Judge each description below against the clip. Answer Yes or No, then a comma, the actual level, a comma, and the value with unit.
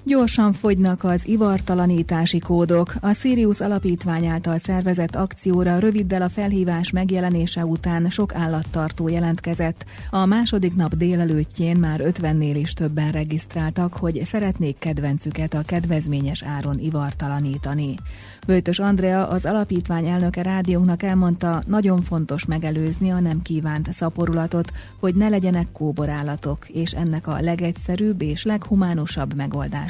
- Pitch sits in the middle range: Yes, medium, 170 Hz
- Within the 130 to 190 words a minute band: No, average, 120 wpm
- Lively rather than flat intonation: No, average, 2.9 semitones